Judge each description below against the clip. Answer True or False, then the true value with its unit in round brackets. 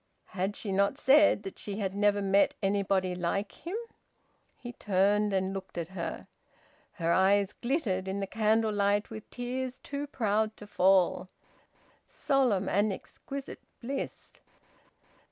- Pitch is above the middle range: True (205 Hz)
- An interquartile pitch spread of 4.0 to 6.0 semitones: False (2.8 semitones)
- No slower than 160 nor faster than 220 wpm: False (135 wpm)